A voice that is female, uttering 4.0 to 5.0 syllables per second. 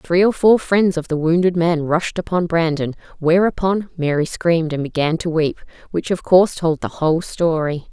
Yes: female; 4.9 syllables/s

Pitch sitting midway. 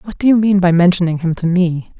Yes: medium, 180 Hz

